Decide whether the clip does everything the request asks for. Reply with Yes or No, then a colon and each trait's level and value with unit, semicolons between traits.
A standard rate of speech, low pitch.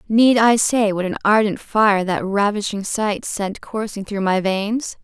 No: average, 180 wpm; high, 205 Hz